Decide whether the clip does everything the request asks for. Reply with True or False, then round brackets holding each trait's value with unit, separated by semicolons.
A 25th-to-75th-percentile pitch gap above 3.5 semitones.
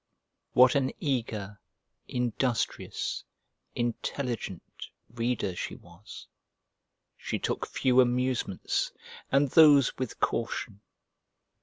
False (3.1 semitones)